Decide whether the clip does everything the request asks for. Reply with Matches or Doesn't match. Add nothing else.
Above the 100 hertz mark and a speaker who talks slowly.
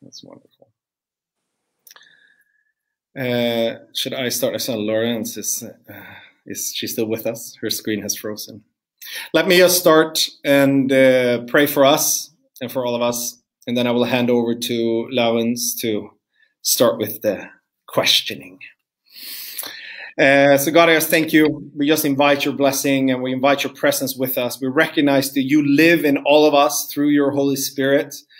Doesn't match